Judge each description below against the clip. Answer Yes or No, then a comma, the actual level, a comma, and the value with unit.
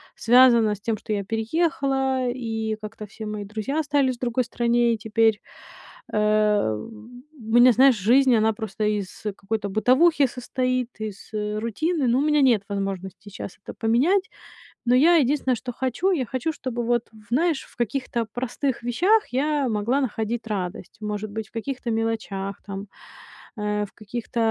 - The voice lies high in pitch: Yes, high, 235 Hz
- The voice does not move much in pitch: No, average, 3.6 semitones